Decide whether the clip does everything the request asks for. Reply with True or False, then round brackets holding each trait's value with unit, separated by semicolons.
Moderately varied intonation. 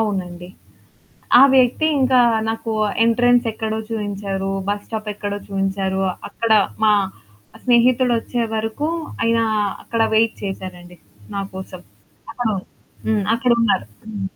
True (3.1 semitones)